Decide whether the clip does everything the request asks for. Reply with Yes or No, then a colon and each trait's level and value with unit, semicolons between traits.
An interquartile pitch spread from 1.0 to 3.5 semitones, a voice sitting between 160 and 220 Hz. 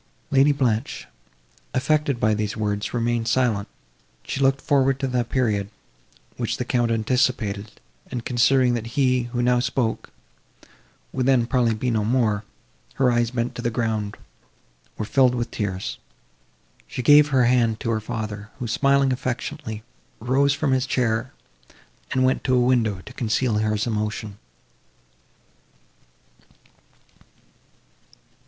No: average, 2.9 semitones; low, 120 Hz